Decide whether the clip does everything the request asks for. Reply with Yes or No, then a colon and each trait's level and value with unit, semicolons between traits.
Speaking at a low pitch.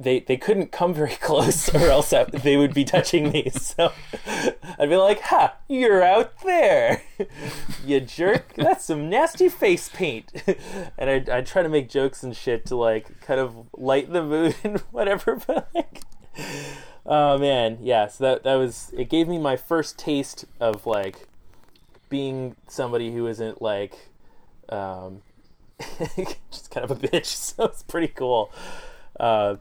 No: medium, 145 Hz